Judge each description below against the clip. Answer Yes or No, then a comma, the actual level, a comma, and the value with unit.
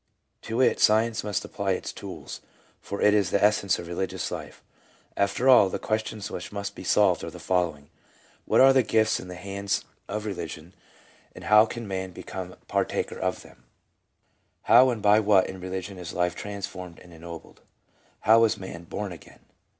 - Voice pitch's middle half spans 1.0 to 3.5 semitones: Yes, average, 2.9 semitones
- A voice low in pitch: Yes, low, 100 Hz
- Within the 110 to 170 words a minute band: No, average, 185 wpm